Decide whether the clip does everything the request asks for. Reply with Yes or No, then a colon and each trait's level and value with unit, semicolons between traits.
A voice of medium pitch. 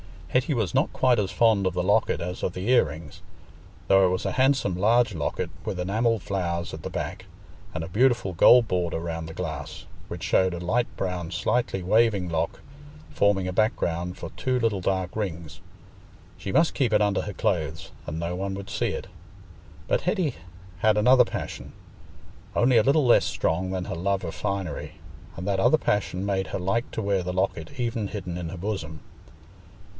No: very low, 95 Hz